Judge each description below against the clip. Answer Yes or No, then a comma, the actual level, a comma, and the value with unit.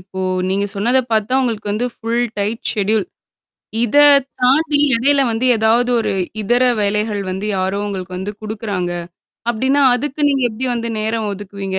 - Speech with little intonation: No, average, 3.4 semitones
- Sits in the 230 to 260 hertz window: No, high, 220 Hz